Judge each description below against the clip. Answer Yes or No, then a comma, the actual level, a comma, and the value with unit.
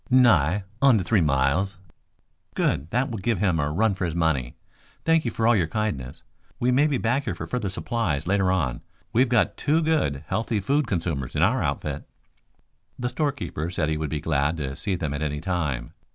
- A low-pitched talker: Yes, very low, 95 Hz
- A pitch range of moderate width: No, wide, 7.6 semitones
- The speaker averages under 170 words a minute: No, average, 195 wpm